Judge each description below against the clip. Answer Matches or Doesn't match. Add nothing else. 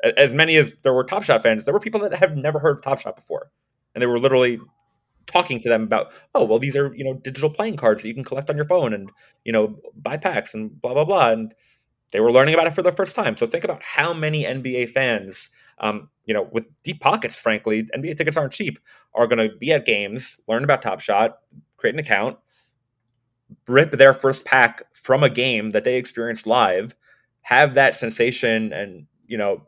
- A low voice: Matches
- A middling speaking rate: Doesn't match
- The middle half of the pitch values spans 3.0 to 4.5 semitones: Doesn't match